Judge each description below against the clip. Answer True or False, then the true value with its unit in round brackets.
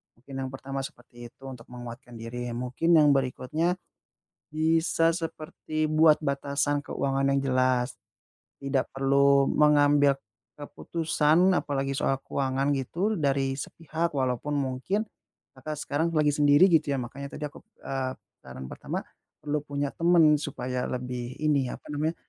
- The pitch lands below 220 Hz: True (140 Hz)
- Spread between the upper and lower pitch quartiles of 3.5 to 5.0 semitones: False (2.8 semitones)